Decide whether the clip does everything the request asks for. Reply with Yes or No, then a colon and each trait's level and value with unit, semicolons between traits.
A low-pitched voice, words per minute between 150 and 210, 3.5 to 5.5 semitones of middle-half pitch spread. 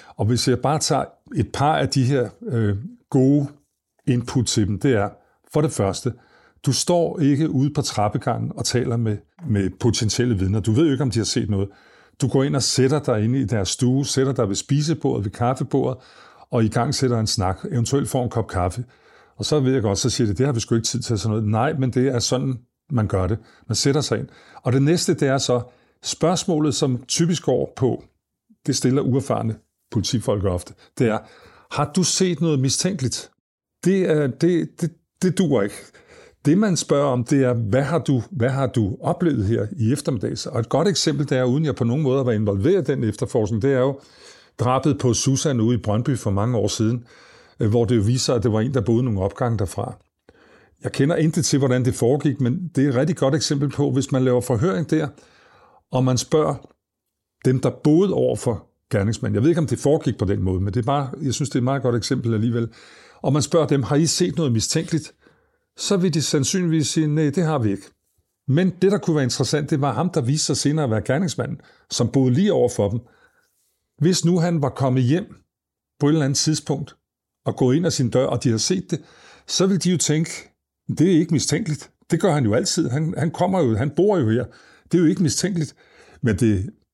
No: low, 130 Hz; fast, 225 wpm; average, 4.6 semitones